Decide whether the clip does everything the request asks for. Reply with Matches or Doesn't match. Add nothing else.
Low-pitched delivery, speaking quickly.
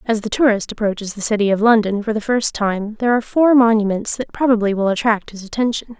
Doesn't match